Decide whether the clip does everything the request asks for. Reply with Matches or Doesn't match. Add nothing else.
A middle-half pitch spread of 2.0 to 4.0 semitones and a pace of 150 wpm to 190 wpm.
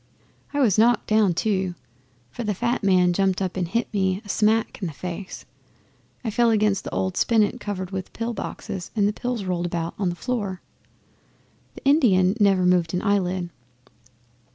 Matches